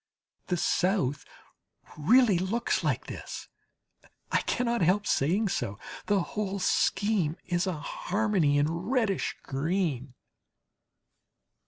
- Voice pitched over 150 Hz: Yes, medium, 185 Hz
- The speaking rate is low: Yes, slow, 105 wpm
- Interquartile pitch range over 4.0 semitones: Yes, average, 5.1 semitones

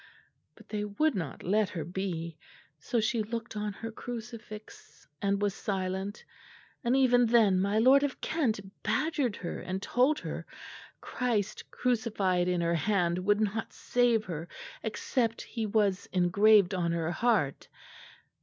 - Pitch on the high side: Yes, high, 210 Hz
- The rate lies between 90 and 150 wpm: Yes, average, 145 wpm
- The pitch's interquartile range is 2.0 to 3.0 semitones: No, average, 3.9 semitones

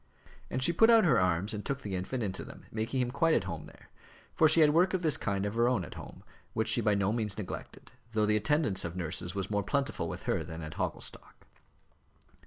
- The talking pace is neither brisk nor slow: No, fast, 235 wpm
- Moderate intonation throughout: No, wide, 6.5 semitones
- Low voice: Yes, low, 110 Hz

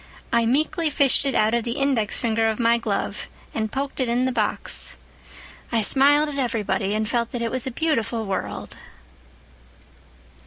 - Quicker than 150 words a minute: Yes, average, 170 wpm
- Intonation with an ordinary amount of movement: Yes, average, 3.5 semitones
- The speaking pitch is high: Yes, high, 235 Hz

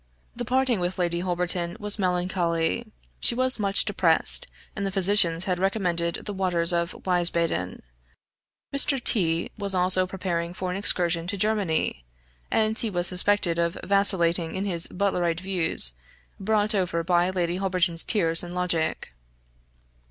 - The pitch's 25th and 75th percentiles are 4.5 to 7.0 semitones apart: No, narrow, 2.6 semitones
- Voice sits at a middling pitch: Yes, medium, 180 Hz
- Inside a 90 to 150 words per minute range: Yes, average, 145 wpm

